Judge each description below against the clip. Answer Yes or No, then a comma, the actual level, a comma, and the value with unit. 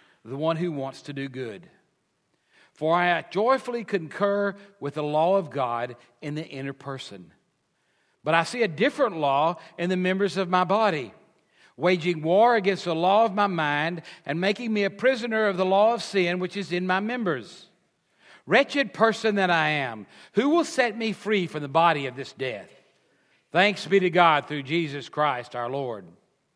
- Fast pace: No, average, 180 wpm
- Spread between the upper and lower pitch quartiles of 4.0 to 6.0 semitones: Yes, average, 5.2 semitones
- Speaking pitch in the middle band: Yes, medium, 180 Hz